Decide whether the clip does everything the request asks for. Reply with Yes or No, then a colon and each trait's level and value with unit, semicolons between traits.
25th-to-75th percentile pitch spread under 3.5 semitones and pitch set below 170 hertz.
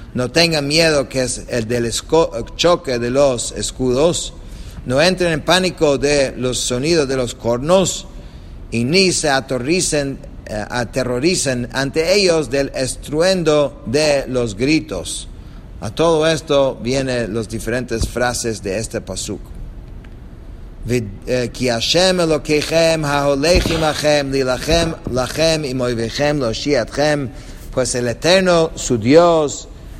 No: average, 4.6 semitones; low, 135 Hz